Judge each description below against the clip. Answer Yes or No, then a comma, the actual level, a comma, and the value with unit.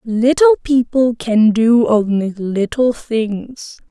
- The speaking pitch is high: Yes, high, 235 Hz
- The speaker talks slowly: Yes, slow, 105 wpm